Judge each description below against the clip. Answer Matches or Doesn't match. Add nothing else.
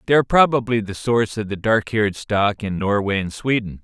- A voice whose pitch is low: Matches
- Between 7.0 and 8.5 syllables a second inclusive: Doesn't match